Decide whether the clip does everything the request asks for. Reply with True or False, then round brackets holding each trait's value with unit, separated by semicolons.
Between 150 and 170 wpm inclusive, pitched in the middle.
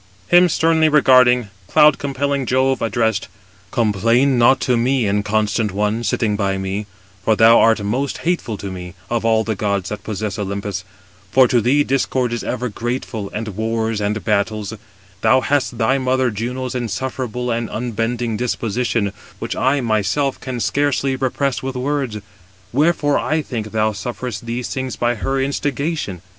False (155 wpm; 120 Hz)